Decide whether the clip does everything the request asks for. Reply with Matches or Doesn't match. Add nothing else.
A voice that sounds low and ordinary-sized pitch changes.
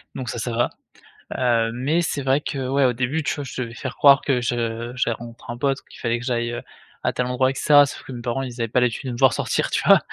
Doesn't match